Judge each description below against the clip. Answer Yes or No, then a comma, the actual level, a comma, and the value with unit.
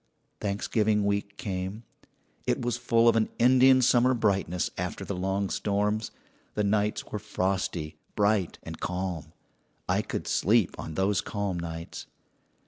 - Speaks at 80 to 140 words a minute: Yes, slow, 135 wpm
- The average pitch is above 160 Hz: No, low, 100 Hz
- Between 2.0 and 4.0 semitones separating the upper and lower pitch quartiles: Yes, average, 2.8 semitones